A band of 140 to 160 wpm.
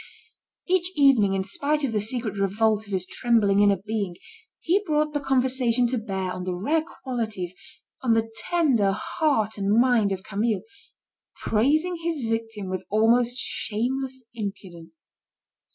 Yes: average, 145 wpm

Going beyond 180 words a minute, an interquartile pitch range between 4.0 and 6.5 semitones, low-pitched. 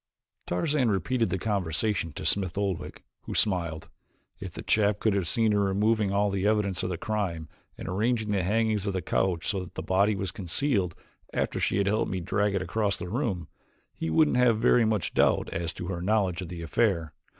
No: average, 200 wpm; average, 3.3 semitones; low, 100 Hz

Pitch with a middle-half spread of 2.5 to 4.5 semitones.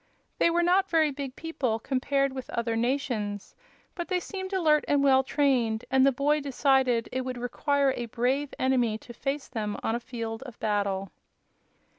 Yes: average, 3.6 semitones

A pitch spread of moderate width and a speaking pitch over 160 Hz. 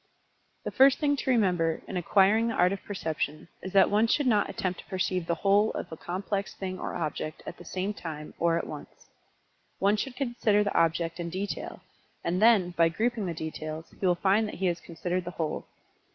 Yes: average, 3.7 semitones; medium, 185 Hz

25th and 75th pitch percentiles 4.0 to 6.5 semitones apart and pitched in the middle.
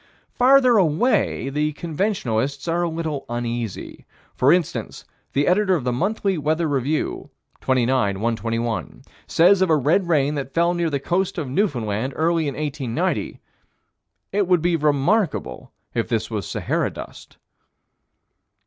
Yes: average, 5.2 semitones; medium, 150 Hz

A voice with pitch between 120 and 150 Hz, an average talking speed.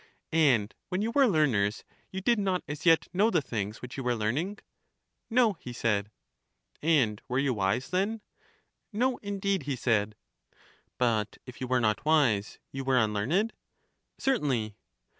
Yes: low, 135 Hz; average, 155 wpm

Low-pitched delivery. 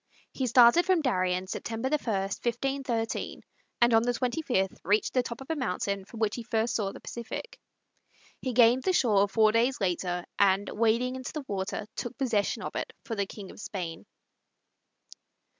No: high, 230 Hz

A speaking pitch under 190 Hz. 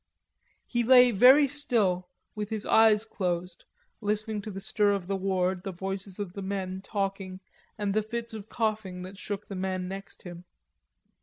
No: high, 200 Hz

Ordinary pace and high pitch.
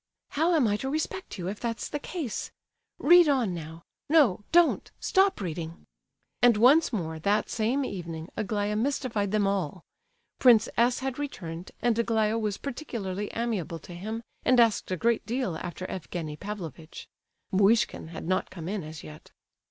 Yes: average, 160 wpm; high, 210 Hz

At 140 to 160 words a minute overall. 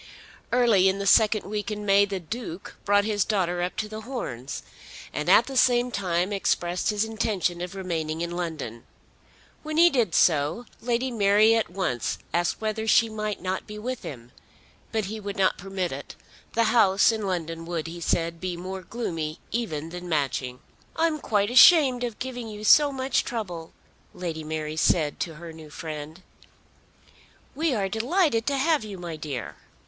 No: average, 175 wpm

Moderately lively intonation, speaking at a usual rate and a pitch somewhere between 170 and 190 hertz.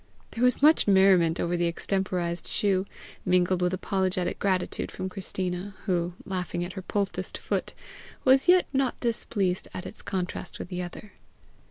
No: narrow, 2.2 semitones; average, 155 wpm; medium, 185 Hz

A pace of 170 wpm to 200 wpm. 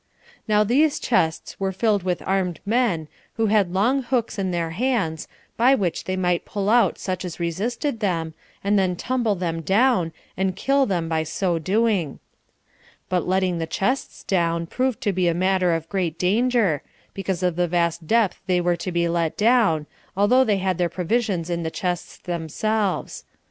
Yes: average, 180 wpm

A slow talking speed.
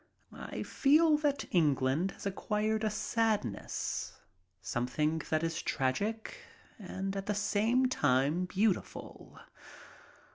Yes: slow, 105 wpm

